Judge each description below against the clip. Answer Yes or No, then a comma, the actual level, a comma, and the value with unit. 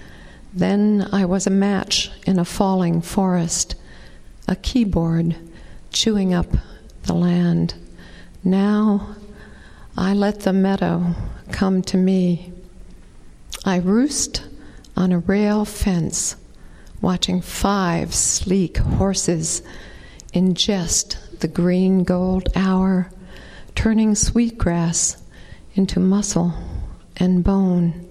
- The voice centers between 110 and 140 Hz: No, medium, 185 Hz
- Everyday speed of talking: No, slow, 95 wpm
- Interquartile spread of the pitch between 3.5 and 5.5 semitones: No, narrow, 2.4 semitones